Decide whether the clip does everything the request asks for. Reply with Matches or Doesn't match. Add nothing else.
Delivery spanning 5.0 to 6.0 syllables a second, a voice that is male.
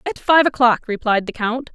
Doesn't match